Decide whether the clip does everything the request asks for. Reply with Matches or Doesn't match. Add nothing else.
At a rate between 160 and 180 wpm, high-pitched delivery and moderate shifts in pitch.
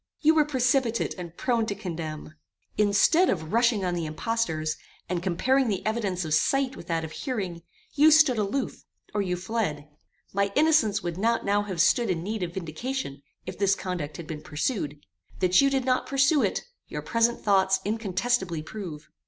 Doesn't match